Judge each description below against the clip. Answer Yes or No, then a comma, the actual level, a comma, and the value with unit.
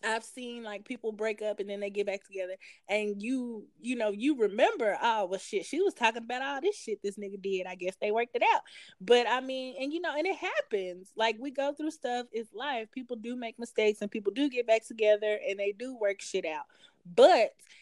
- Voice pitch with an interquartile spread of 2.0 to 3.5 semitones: No, average, 4.4 semitones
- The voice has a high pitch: Yes, high, 225 Hz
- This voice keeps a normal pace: No, fast, 235 wpm